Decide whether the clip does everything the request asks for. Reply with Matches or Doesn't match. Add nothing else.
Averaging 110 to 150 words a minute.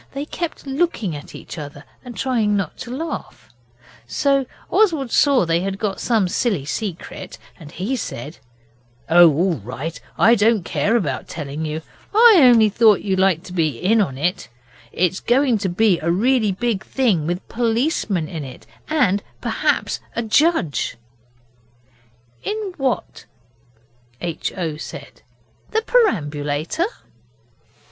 Matches